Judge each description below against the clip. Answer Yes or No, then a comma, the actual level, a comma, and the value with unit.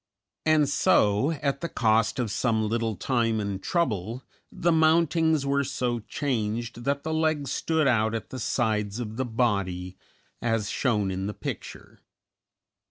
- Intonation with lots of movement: No, average, 4.7 semitones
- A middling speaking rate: Yes, average, 150 wpm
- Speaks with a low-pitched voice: Yes, low, 120 Hz